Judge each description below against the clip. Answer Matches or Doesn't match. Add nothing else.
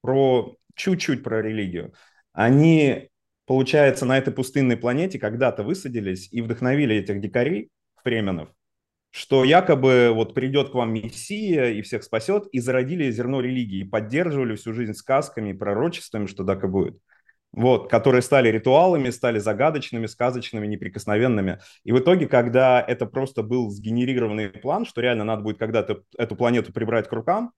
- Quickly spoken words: Doesn't match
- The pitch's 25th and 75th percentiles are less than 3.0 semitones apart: Doesn't match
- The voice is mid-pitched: Doesn't match